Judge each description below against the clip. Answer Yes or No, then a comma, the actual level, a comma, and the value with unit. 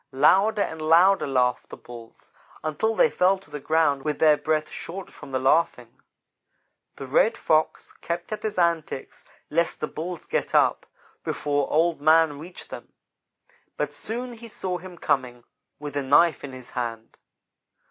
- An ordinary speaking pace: Yes, average, 160 wpm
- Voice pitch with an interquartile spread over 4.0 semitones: Yes, average, 4.4 semitones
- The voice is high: No, medium, 155 Hz